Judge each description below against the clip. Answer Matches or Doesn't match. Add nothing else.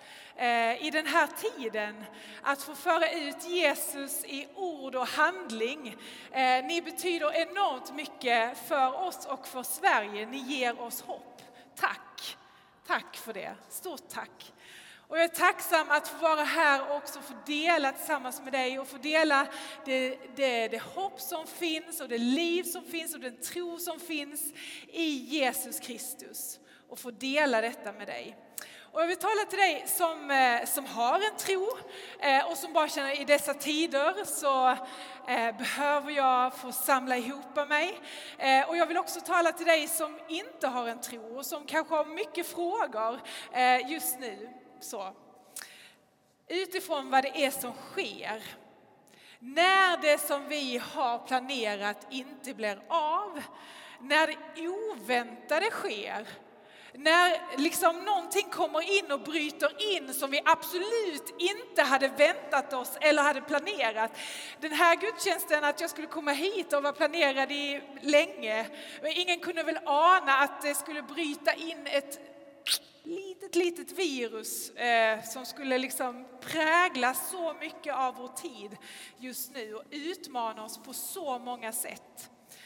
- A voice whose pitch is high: Matches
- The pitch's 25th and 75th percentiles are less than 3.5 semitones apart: Doesn't match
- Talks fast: Doesn't match